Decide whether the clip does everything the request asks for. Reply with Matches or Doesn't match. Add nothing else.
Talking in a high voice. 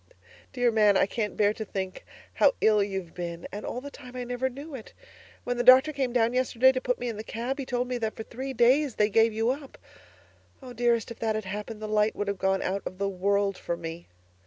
Matches